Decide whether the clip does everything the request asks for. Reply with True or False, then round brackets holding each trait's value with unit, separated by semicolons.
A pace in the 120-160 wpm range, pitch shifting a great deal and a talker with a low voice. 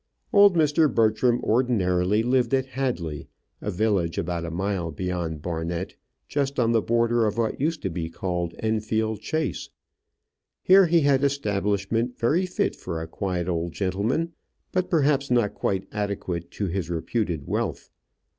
True (155 wpm; 6.6 semitones; 110 Hz)